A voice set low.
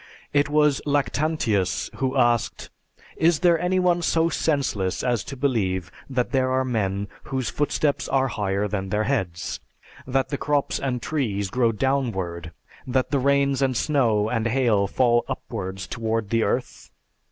Yes: low, 125 Hz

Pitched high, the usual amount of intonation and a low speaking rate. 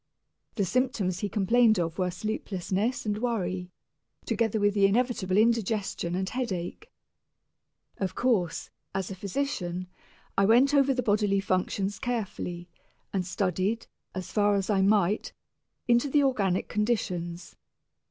Yes: high, 205 Hz; average, 3.9 semitones; slow, 130 wpm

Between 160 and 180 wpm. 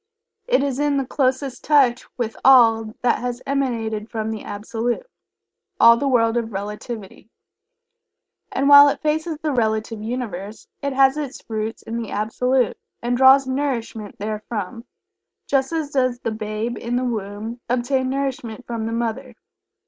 No: average, 150 wpm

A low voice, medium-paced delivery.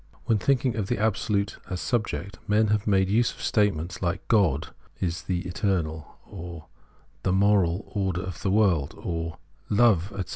Yes: very low, 95 Hz; average, 175 wpm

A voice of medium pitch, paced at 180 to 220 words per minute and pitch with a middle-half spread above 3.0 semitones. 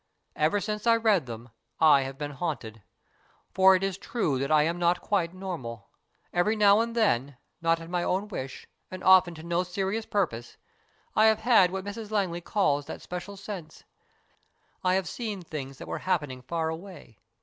Yes: medium, 180 Hz; average, 185 wpm; average, 5.0 semitones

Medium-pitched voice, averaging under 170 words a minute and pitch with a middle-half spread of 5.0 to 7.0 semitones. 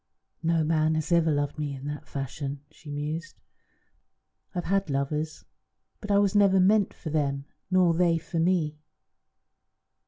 No: medium, 160 Hz; average, 150 wpm; average, 3.4 semitones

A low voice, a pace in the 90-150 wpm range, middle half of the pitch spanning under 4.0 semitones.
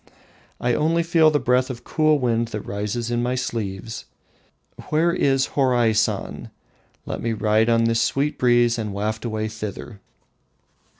Yes: low, 120 Hz; average, 145 wpm; average, 3.3 semitones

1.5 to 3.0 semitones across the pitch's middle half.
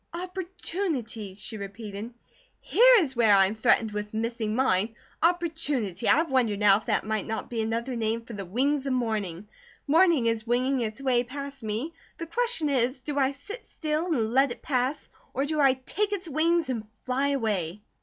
No: wide, 5.5 semitones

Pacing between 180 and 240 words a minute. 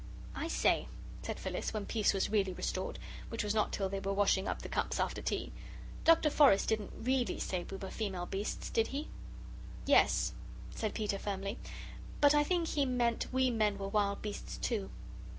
Yes: average, 185 wpm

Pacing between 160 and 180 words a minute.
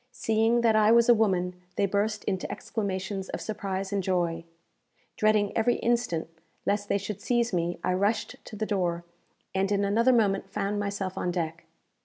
Yes: average, 175 wpm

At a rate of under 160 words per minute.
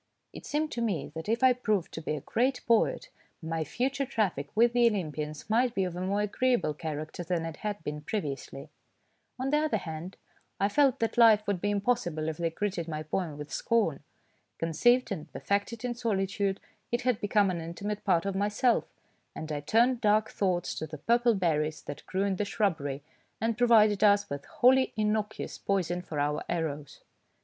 No: average, 190 wpm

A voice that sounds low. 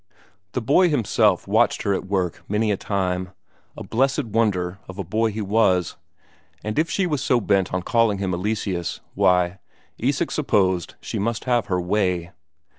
Yes: low, 100 Hz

